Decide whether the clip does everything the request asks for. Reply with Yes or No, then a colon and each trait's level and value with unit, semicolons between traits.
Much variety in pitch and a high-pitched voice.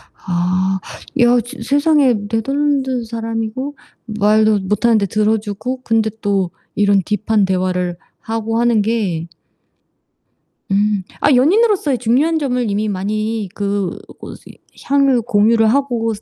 No: average, 3.6 semitones; high, 220 Hz